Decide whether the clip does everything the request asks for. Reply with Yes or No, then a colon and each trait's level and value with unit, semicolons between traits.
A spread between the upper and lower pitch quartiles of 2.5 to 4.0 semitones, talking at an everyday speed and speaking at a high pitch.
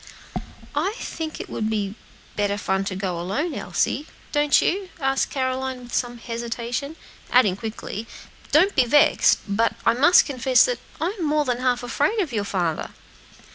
No: wide, 5.4 semitones; average, 160 wpm; very high, 250 Hz